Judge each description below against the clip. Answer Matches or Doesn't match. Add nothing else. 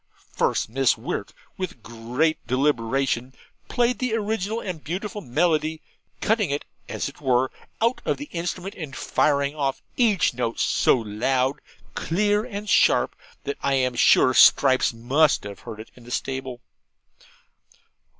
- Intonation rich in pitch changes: Matches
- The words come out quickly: Doesn't match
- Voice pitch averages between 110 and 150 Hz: Matches